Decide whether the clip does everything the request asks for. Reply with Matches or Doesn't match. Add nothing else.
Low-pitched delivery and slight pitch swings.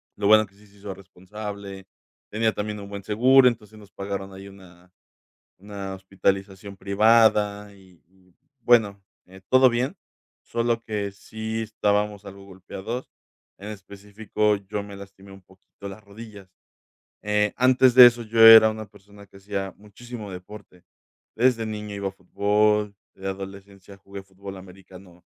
Matches